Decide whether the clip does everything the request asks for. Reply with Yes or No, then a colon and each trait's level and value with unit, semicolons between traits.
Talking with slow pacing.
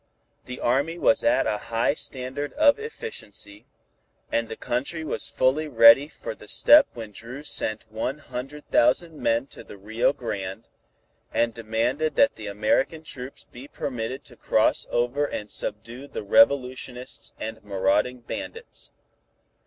No: average, 145 wpm